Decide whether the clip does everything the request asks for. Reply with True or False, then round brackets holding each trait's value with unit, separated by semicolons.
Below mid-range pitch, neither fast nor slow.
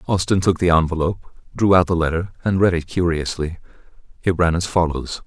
True (85 Hz; 180 wpm)